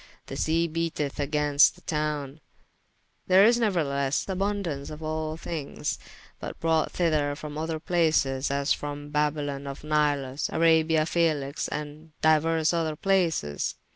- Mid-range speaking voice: Yes, medium, 155 Hz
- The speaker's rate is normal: No, slow, 130 wpm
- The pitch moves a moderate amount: No, narrow, 2.2 semitones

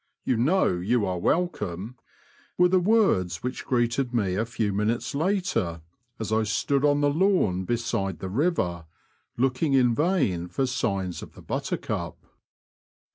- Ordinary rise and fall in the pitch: No, wide, 7.4 semitones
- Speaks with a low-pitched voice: Yes, low, 120 Hz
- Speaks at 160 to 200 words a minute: No, average, 145 wpm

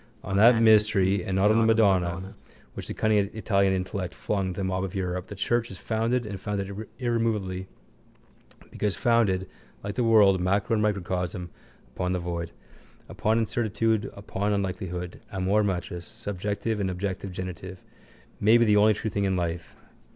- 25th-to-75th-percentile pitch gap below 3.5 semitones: Yes, average, 2.8 semitones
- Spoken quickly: No, average, 165 wpm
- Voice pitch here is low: Yes, low, 100 Hz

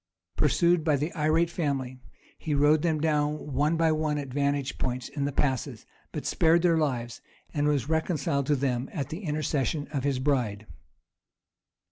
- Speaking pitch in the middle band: Yes, medium, 145 Hz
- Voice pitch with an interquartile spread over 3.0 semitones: No, narrow, 2.4 semitones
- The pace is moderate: Yes, average, 165 wpm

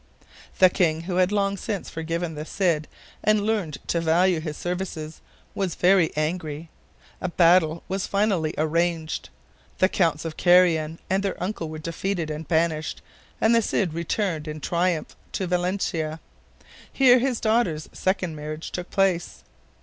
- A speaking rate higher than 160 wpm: No, average, 150 wpm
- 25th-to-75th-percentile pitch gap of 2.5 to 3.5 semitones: Yes, average, 3.2 semitones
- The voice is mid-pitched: Yes, medium, 175 Hz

